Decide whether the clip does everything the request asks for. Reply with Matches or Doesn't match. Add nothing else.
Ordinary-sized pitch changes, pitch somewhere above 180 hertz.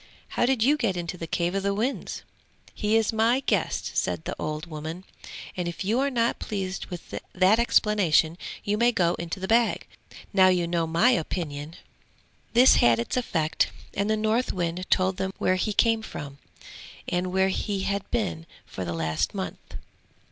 Matches